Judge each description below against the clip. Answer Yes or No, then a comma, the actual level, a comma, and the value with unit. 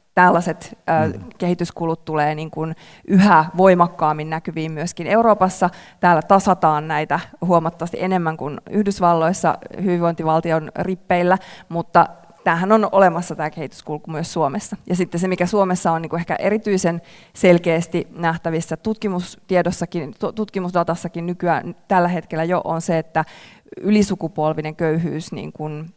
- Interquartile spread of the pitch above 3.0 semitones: No, narrow, 2.6 semitones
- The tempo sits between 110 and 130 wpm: Yes, average, 120 wpm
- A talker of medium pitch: Yes, medium, 170 Hz